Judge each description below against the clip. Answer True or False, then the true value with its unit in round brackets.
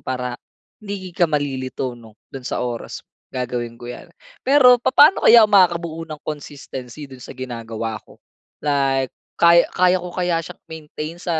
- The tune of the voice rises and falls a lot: True (5.8 semitones)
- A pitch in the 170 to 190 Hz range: False (150 Hz)